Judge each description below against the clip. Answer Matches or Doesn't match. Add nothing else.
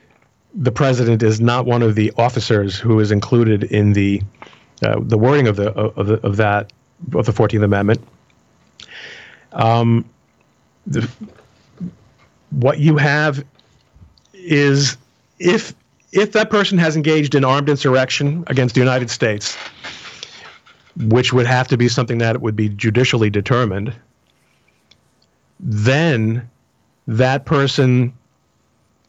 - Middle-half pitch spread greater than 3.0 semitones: Matches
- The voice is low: Matches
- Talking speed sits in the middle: Doesn't match